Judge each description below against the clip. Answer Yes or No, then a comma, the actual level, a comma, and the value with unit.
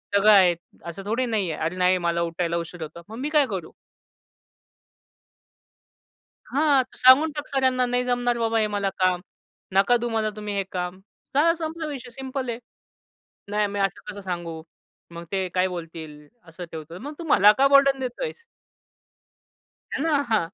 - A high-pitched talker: Yes, high, 210 Hz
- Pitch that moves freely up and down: Yes, wide, 6.5 semitones